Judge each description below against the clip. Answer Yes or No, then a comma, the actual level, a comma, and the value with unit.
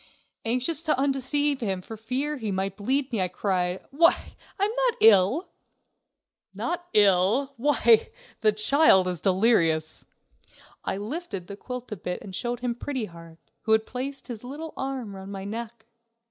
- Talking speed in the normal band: Yes, average, 160 wpm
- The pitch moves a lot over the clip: Yes, wide, 5.9 semitones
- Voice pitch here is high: Yes, high, 230 Hz